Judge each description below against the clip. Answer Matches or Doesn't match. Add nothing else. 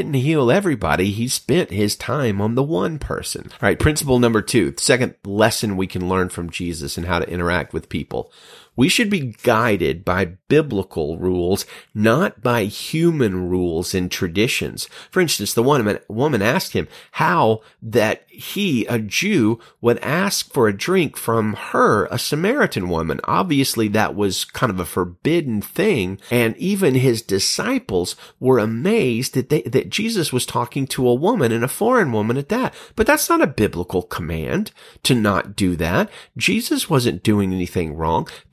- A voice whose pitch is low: Matches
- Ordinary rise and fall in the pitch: Doesn't match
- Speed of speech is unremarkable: Matches